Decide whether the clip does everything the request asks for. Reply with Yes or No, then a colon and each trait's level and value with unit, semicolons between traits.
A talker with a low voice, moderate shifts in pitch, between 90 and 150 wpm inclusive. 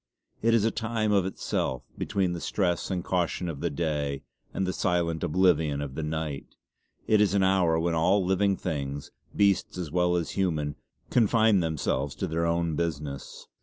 No: very low, 85 Hz; average, 3.7 semitones; average, 175 wpm